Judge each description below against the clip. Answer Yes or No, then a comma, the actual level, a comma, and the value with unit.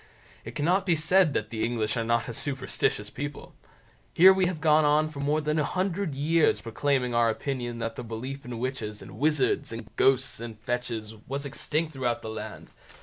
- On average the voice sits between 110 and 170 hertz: Yes, low, 135 Hz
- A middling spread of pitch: Yes, average, 4.7 semitones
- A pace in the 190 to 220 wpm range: Yes, average, 195 wpm